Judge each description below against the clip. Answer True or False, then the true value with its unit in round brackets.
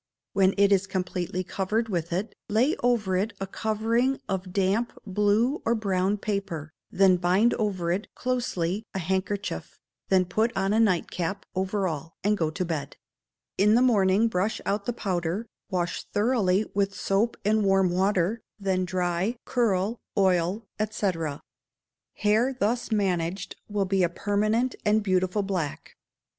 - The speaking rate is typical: True (150 wpm)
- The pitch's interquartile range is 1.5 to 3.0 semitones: True (2.7 semitones)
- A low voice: False (195 Hz)